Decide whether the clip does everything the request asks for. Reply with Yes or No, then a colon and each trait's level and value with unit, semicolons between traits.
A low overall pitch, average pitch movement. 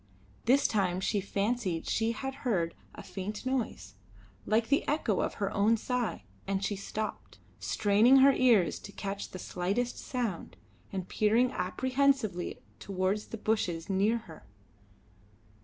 No: high, 210 Hz; average, 4.1 semitones